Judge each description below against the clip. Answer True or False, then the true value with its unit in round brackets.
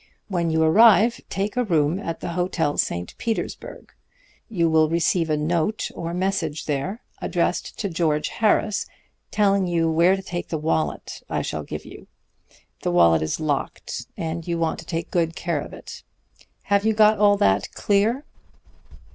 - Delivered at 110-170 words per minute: True (165 wpm)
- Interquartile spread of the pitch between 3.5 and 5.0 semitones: True (4.0 semitones)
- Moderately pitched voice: True (170 Hz)